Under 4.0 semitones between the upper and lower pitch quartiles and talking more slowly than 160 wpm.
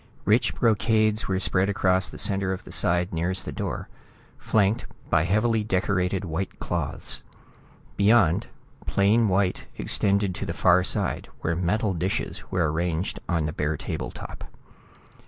Yes: average, 2.9 semitones; average, 145 wpm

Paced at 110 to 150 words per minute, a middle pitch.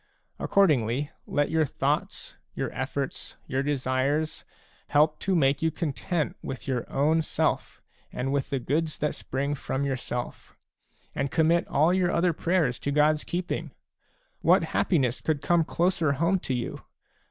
Yes: average, 145 wpm; medium, 150 Hz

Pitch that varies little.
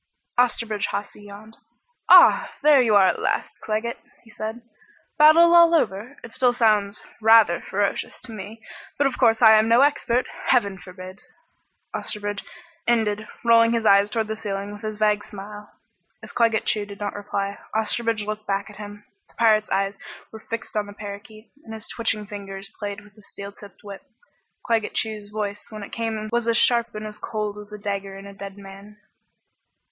Yes: narrow, 2.0 semitones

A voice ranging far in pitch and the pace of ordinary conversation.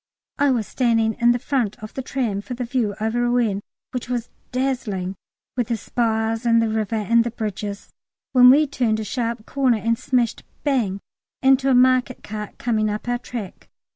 No: narrow, 2.6 semitones; average, 185 wpm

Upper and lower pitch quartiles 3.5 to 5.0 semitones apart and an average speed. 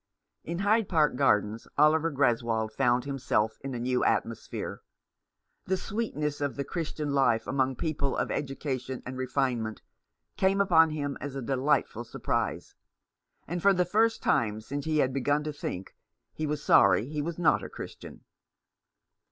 Yes: average, 4.1 semitones; average, 160 wpm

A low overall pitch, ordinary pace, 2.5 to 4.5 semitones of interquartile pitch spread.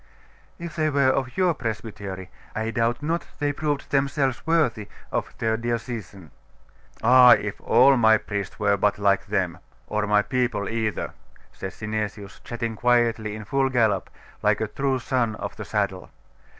Yes: low, 115 Hz; average, 155 wpm; average, 4.1 semitones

